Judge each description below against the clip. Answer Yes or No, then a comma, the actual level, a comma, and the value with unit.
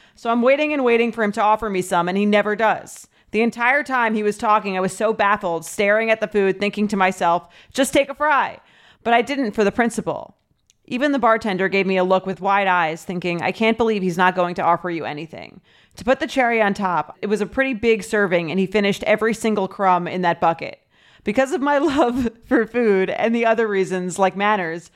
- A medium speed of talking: No, fast, 230 wpm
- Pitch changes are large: No, average, 3.7 semitones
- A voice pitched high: Yes, high, 210 Hz